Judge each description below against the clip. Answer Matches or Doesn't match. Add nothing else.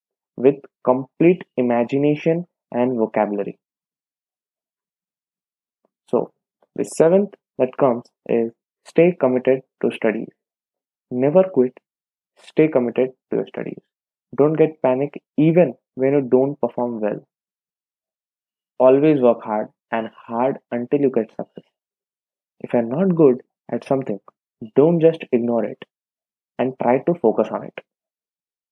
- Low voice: Matches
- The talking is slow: Matches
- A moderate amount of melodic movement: Matches